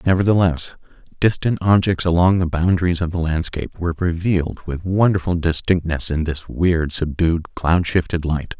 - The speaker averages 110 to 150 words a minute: Yes, average, 145 wpm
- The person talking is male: Yes, male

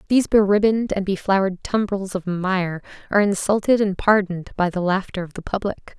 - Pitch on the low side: No, high, 195 Hz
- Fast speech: No, average, 190 wpm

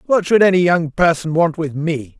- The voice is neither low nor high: Yes, medium, 165 Hz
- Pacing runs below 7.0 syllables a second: Yes, 4.9 syllables/s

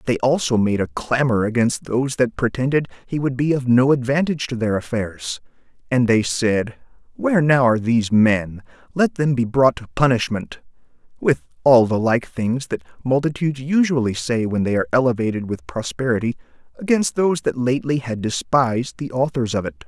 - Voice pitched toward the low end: Yes, low, 125 Hz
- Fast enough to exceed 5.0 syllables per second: Yes, 5.4 syllables/s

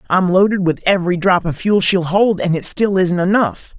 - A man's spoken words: Yes, male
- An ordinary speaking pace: No, fast, 220 wpm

